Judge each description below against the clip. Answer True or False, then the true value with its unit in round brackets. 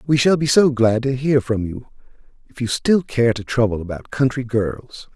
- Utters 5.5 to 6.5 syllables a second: False (4.8 syllables/s)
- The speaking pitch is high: False (125 Hz)